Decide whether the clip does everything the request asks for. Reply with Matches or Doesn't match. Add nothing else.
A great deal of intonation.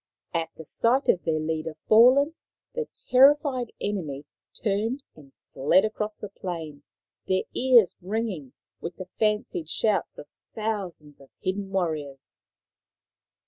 Matches